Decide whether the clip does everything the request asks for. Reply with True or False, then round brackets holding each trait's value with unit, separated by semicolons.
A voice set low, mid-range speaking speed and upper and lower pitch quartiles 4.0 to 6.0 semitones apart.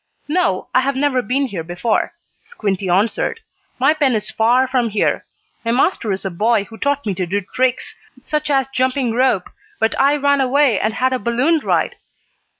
False (250 Hz; 185 wpm; 4.5 semitones)